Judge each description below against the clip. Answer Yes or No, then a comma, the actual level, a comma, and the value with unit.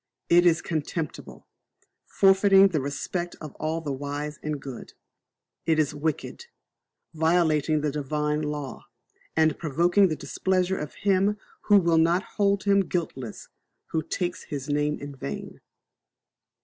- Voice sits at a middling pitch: Yes, medium, 160 Hz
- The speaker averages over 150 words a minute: No, slow, 135 wpm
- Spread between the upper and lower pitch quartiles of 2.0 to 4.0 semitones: Yes, average, 3.3 semitones